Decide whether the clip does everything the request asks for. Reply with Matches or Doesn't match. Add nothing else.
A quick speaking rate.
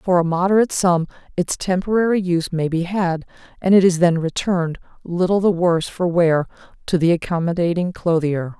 Doesn't match